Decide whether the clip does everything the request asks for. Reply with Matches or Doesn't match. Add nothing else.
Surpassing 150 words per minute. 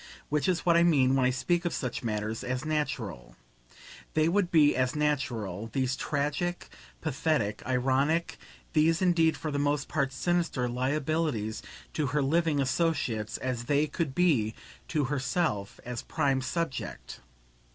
Doesn't match